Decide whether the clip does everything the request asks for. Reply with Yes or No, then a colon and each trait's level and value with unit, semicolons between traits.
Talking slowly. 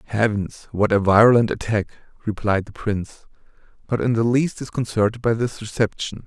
No: average, 155 wpm